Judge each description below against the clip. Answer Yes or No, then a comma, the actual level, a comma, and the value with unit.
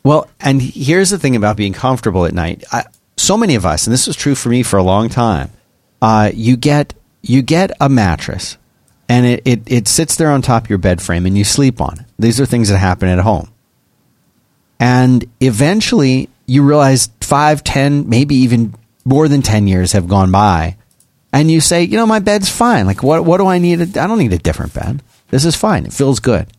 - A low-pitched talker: Yes, low, 125 Hz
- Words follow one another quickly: Yes, fast, 220 wpm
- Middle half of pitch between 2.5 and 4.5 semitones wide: No, wide, 5.4 semitones